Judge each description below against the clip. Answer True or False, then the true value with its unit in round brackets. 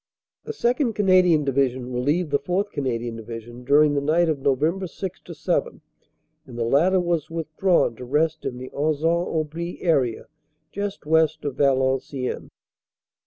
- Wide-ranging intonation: False (4.8 semitones)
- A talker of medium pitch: True (150 Hz)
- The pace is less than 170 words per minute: True (150 wpm)